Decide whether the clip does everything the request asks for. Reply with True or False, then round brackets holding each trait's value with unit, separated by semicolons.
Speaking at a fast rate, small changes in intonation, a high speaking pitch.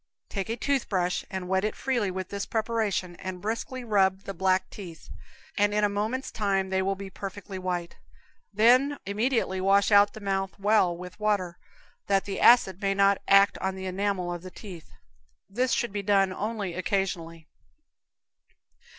False (170 wpm; 2.0 semitones; 195 Hz)